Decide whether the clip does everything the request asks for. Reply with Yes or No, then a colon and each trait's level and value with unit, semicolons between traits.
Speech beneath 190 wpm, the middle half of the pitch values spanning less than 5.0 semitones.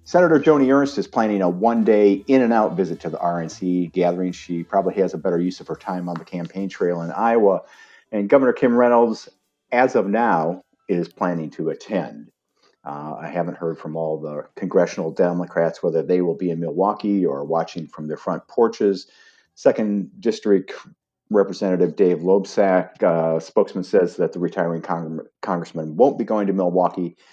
Yes: average, 170 wpm; average, 3.8 semitones